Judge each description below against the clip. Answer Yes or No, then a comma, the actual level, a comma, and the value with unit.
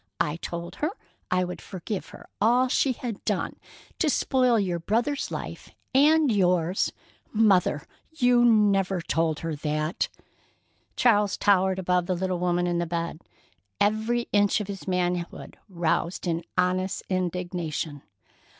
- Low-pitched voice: No, medium, 185 Hz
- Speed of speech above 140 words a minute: No, slow, 135 wpm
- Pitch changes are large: No, average, 3.9 semitones